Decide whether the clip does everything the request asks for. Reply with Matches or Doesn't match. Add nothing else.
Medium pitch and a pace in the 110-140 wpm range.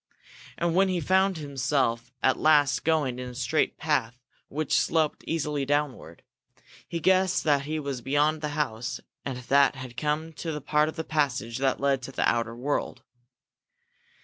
Doesn't match